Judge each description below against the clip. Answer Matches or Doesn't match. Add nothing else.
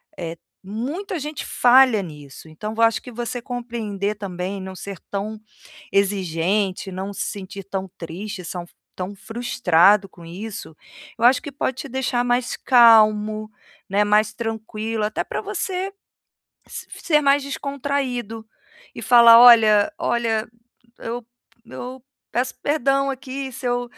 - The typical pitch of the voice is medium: Doesn't match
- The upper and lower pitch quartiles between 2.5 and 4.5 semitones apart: Matches